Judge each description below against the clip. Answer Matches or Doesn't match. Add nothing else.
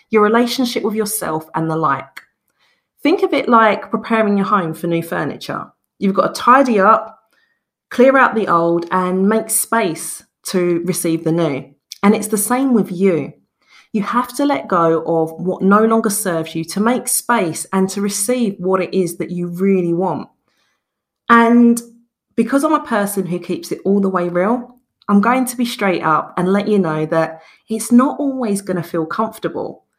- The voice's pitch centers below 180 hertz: Doesn't match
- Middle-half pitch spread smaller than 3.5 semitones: Doesn't match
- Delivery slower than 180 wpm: Doesn't match